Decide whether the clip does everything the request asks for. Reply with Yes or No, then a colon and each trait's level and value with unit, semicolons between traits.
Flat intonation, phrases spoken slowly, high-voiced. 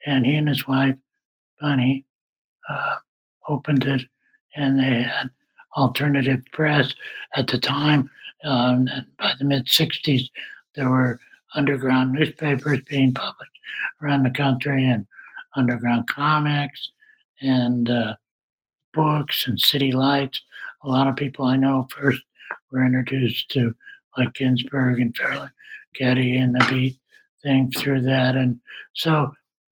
No: narrow, 1.9 semitones; slow, 130 wpm; low, 135 Hz